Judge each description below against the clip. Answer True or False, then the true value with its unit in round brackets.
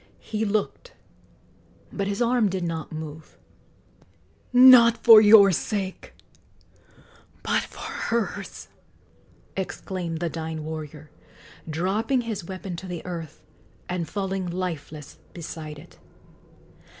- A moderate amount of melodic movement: True (4.8 semitones)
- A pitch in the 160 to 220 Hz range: True (185 Hz)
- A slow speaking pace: True (105 wpm)